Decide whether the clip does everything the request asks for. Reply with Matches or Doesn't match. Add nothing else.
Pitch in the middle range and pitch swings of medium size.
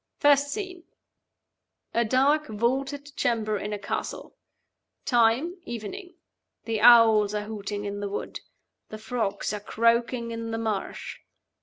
Doesn't match